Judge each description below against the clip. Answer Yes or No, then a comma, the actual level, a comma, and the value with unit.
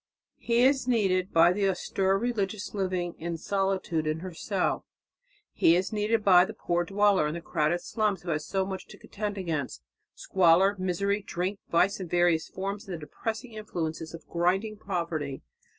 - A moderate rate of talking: Yes, average, 170 wpm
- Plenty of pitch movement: No, average, 3.0 semitones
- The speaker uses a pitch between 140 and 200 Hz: Yes, high, 190 Hz